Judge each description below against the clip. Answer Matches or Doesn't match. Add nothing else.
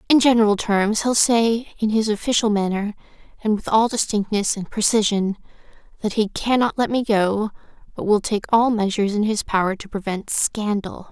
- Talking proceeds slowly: Doesn't match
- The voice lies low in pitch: Doesn't match